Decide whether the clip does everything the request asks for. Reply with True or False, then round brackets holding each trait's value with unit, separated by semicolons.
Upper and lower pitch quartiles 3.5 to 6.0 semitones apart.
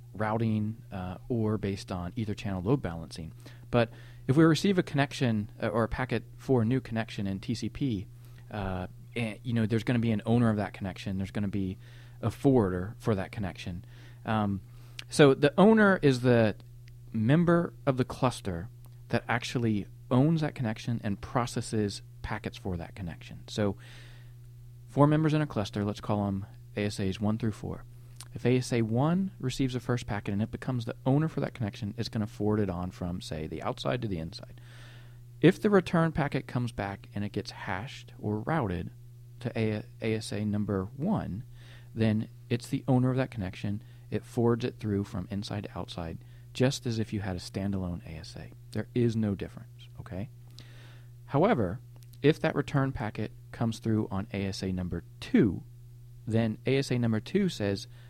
False (2.8 semitones)